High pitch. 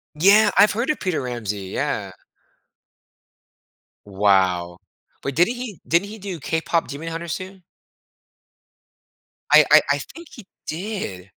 No: medium, 165 Hz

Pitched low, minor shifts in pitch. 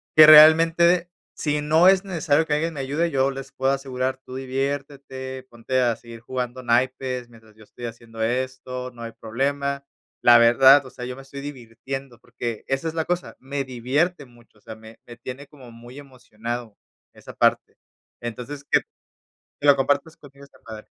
No: low, 130 Hz; average, 3.0 semitones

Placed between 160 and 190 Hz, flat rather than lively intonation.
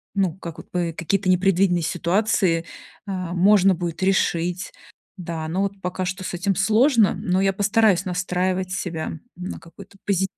Yes: medium, 185 Hz; narrow, 1.9 semitones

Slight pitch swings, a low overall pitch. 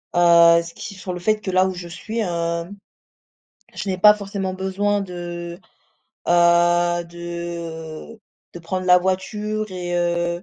No: narrow, 1.7 semitones; medium, 175 Hz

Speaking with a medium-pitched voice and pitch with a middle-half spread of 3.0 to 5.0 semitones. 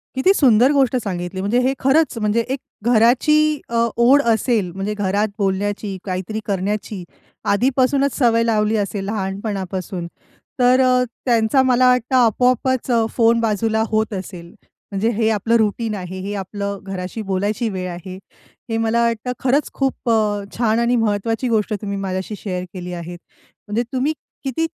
No: high, 220 Hz; average, 4.0 semitones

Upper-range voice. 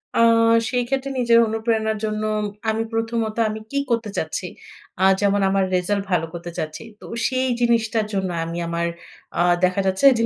Yes: high, 215 Hz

